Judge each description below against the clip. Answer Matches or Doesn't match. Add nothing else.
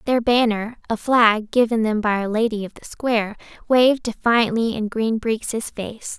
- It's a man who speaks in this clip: Doesn't match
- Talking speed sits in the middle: Matches